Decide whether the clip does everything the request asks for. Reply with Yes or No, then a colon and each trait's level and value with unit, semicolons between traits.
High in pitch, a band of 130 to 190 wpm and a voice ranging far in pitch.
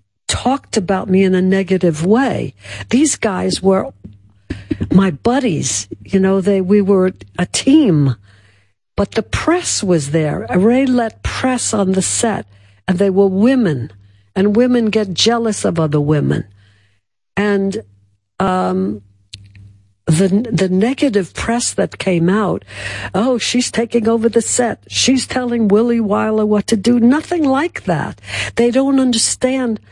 Yes: high, 195 Hz; average, 140 wpm; wide, 8.2 semitones